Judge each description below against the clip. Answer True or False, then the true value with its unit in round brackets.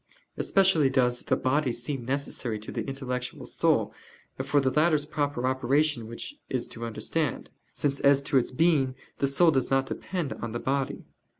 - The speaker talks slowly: False (170 wpm)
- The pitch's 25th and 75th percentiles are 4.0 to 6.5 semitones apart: False (2.8 semitones)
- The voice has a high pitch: False (135 Hz)